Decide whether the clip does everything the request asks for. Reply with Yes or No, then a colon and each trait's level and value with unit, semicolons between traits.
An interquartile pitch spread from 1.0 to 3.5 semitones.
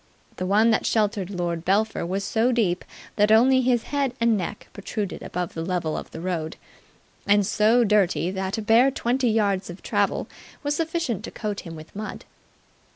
No: average, 4.0 semitones